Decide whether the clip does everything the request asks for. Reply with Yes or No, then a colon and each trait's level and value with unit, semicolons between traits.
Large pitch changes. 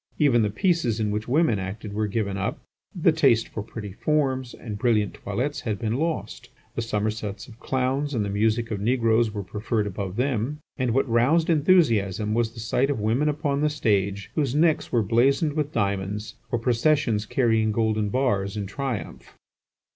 No: average, 4.5 semitones